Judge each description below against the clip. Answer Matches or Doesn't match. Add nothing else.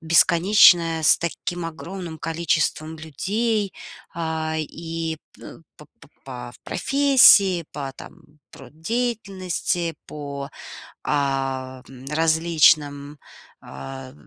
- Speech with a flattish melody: Doesn't match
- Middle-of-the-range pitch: Matches